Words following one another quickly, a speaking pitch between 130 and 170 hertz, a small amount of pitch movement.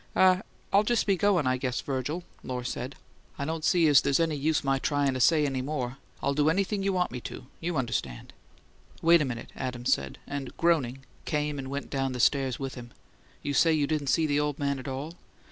No: fast, 220 wpm; medium, 140 Hz; average, 3.6 semitones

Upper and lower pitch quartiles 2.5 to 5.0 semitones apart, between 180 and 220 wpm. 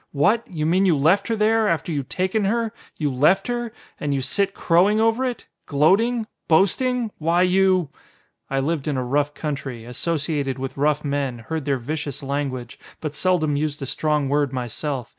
No: wide, 5.6 semitones; average, 185 wpm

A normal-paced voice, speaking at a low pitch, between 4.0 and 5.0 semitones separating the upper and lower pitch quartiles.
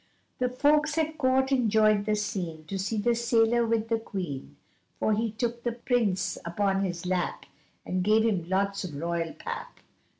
No: average, 170 wpm; high, 215 Hz; average, 4.3 semitones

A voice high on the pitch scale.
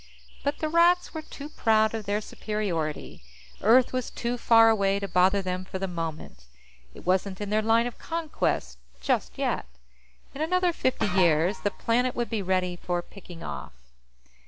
Yes: high, 210 Hz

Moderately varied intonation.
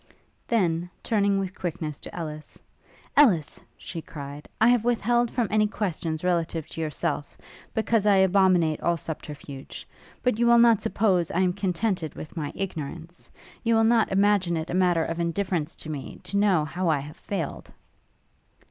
Yes: average, 4.5 semitones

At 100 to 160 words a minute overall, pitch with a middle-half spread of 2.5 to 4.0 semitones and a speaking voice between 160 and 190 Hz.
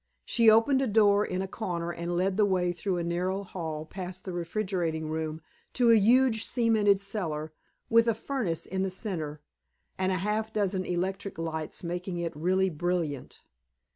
No: average, 170 wpm; average, 3.6 semitones; medium, 185 Hz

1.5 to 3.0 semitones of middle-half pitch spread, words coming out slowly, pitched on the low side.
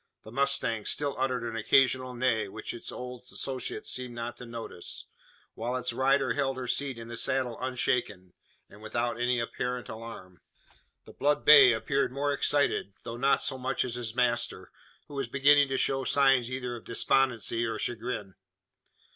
No: narrow, 2.4 semitones; average, 170 wpm; low, 125 Hz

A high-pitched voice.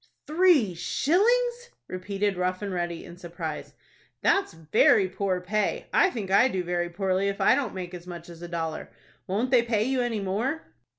Yes: high, 195 Hz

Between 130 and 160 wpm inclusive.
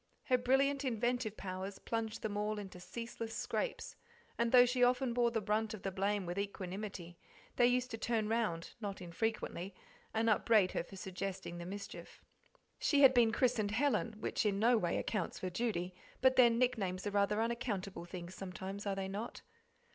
No: average, 175 wpm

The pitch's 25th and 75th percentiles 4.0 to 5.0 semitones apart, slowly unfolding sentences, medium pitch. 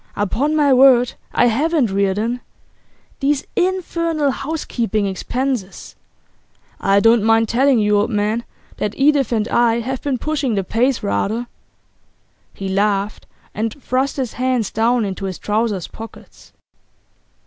No: average, 4.5 semitones; slow, 130 wpm; high, 235 Hz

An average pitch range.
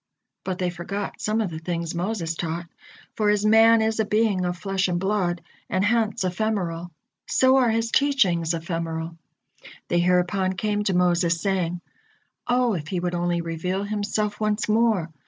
Yes: average, 3.6 semitones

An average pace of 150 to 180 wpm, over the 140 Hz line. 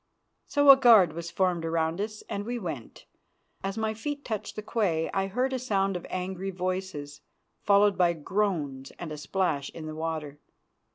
Yes: average, 175 wpm; medium, 185 Hz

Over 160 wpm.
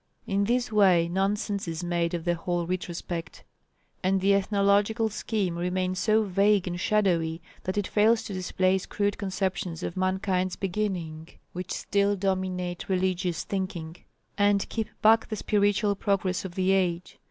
No: average, 150 wpm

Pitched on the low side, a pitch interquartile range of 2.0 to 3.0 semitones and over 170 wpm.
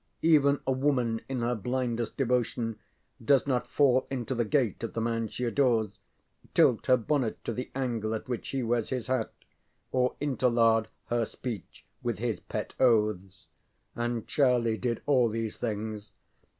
No: low, 120 Hz; narrow, 2.4 semitones; average, 160 wpm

